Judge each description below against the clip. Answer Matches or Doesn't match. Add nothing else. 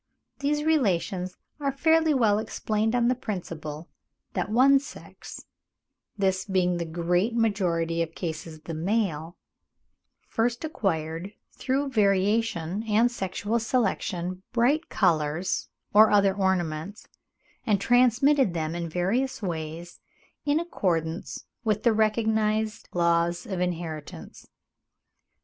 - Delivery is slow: Matches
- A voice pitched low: Doesn't match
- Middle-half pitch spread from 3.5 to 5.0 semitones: Doesn't match